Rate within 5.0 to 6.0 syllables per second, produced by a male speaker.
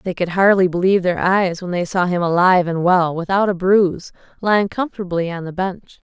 No: 5.7 syllables/s; female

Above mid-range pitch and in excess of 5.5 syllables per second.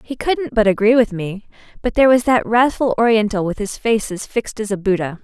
Yes: high, 220 Hz; 5.7 syllables/s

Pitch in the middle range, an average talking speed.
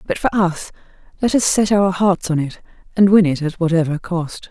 No: medium, 180 Hz; fast, 215 wpm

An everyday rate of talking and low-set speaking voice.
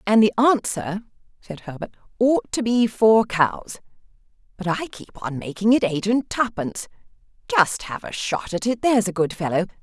No: average, 175 wpm; high, 210 Hz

